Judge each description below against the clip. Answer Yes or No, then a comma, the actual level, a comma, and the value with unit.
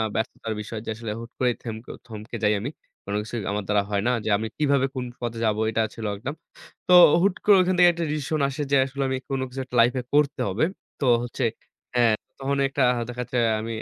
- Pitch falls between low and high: No, low, 125 Hz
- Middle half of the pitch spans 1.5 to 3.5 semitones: No, average, 3.9 semitones